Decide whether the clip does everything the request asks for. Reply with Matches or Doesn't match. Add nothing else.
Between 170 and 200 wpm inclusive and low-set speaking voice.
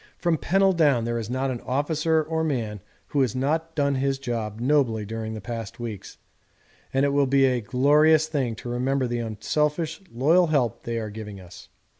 Matches